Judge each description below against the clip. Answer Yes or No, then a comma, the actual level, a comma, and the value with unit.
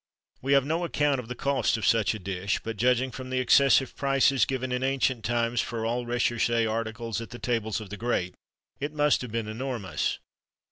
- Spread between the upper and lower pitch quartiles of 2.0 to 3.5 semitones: Yes, average, 2.8 semitones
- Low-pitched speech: Yes, low, 120 Hz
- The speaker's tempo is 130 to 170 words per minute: No, average, 200 wpm